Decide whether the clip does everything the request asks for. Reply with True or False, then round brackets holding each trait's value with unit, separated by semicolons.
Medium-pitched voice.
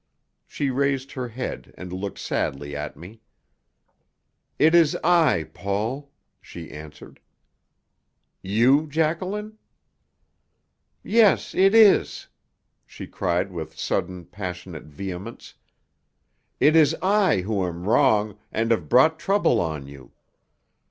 False (115 Hz)